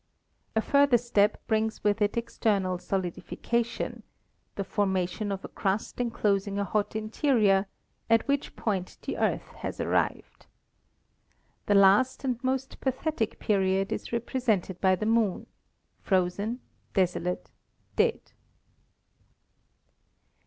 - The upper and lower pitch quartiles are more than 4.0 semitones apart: No, average, 3.4 semitones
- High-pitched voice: Yes, high, 210 Hz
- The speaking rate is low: Yes, slow, 115 wpm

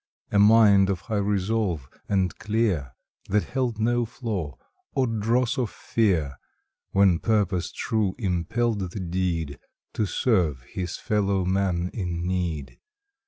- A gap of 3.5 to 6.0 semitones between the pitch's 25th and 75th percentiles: Yes, average, 3.9 semitones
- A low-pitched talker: Yes, low, 100 Hz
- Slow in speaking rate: Yes, slow, 125 wpm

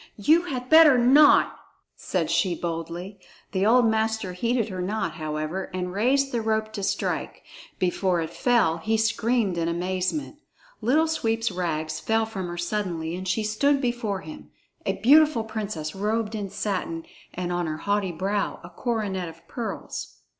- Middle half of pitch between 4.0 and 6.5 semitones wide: Yes, average, 4.5 semitones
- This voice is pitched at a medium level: No, high, 205 Hz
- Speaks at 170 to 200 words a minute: No, average, 160 wpm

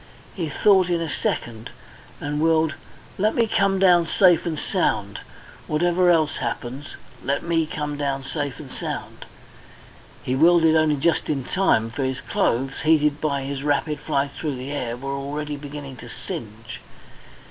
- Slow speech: No, average, 160 wpm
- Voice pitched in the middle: Yes, medium, 150 Hz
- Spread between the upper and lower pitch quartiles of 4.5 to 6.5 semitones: No, average, 3.3 semitones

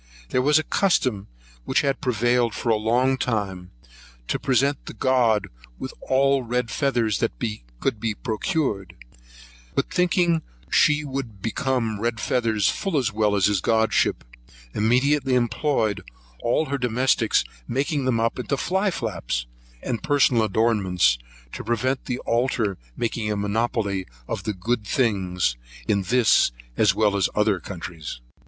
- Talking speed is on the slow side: No, average, 150 wpm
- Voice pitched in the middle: No, low, 115 Hz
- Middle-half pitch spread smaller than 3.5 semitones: No, average, 4.0 semitones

